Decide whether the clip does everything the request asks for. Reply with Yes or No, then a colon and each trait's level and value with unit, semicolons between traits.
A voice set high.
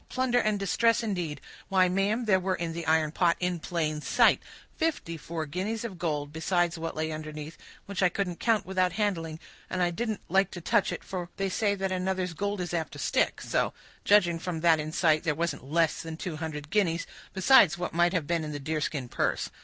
No: medium, 175 Hz